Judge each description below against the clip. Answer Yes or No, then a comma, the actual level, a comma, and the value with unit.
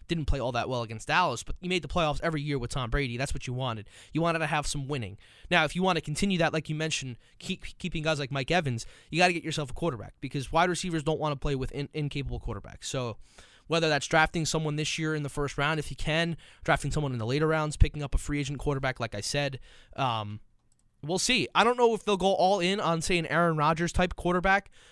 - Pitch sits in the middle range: Yes, medium, 150 Hz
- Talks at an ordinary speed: No, fast, 260 wpm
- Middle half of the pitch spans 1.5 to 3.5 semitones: No, average, 3.9 semitones